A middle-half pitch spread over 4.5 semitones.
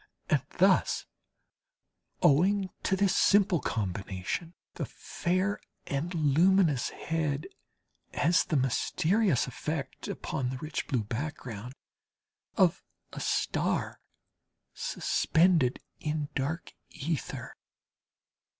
Yes: average, 5.1 semitones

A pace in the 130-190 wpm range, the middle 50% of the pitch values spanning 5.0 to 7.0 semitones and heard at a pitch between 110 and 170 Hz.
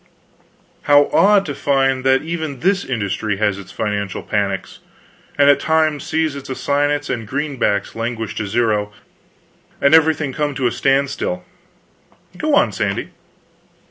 Yes: average, 140 wpm; average, 5.3 semitones; low, 135 Hz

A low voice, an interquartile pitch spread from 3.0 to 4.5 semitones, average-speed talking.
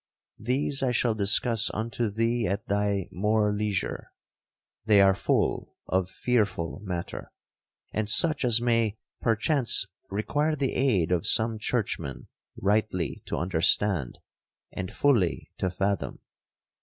No: low, 105 Hz; average, 3.5 semitones; slow, 120 wpm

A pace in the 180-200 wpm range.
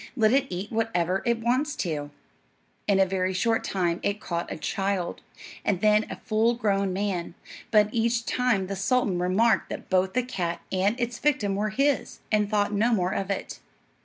Yes: average, 185 wpm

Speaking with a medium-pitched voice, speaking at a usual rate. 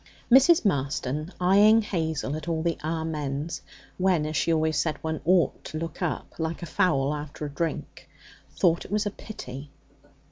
Yes: medium, 160 Hz; average, 165 wpm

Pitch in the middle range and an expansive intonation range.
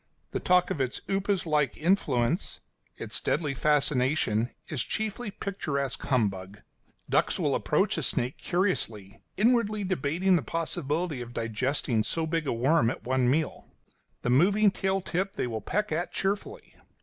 Yes: medium, 155 Hz; wide, 7.1 semitones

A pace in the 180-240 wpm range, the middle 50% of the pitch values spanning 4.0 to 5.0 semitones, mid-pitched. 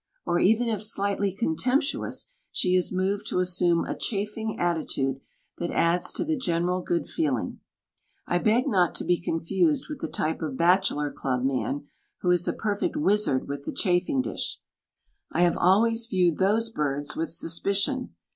No: average, 165 wpm; average, 4.4 semitones; medium, 180 Hz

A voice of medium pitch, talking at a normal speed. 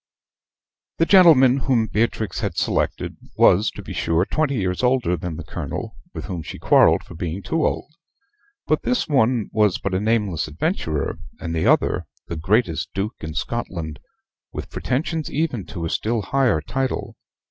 No: low, 105 Hz; average, 165 wpm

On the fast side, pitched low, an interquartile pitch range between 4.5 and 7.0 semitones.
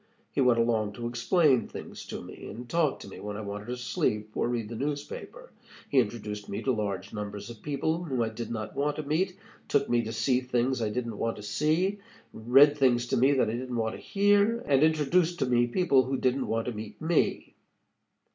Yes: fast, 220 wpm; low, 125 Hz; average, 4.8 semitones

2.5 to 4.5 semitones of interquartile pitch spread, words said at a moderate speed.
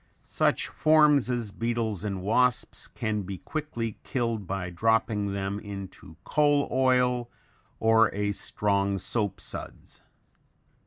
No: average, 3.8 semitones; slow, 115 wpm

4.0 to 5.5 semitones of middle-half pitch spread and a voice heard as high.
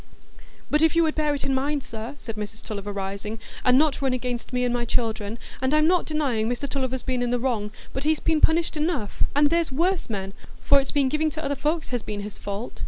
Yes: average, 5.1 semitones; very high, 260 Hz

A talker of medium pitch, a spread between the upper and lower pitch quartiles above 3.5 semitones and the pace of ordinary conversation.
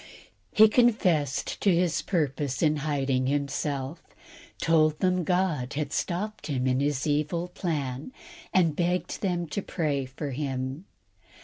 No: medium, 150 Hz; average, 4.3 semitones; slow, 130 wpm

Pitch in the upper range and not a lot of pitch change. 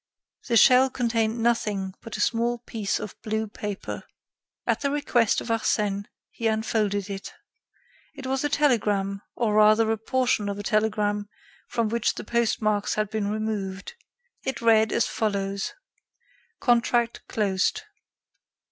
Yes: high, 220 Hz; narrow, 2.3 semitones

